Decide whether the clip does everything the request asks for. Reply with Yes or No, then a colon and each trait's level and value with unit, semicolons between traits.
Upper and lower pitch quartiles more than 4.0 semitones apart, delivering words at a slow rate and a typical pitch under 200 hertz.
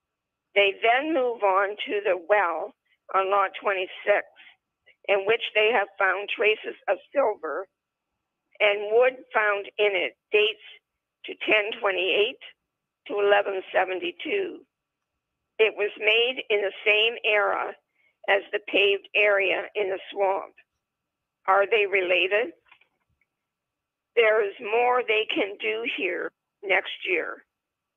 No: average, 4.9 semitones; slow, 115 wpm; high, 210 Hz